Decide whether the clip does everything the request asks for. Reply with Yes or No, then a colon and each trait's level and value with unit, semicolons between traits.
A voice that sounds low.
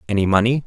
Yes: low, 110 Hz